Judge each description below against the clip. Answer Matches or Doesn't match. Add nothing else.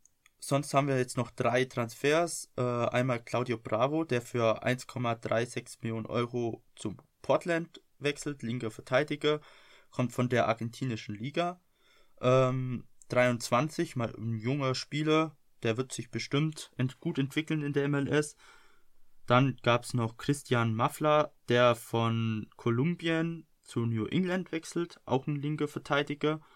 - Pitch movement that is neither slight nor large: Matches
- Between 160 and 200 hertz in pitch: Doesn't match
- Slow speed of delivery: Doesn't match